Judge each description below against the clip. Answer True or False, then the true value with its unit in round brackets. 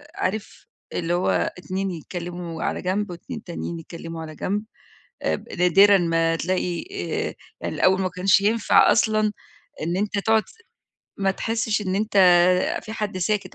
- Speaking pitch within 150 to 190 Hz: True (185 Hz)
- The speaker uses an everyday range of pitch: True (3.2 semitones)